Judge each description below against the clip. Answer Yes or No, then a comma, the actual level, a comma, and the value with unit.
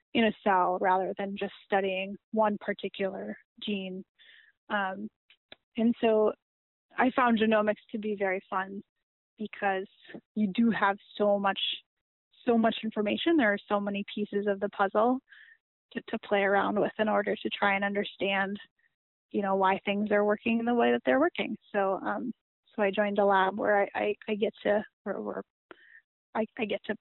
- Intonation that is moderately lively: No, narrow, 1.8 semitones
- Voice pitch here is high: Yes, high, 205 Hz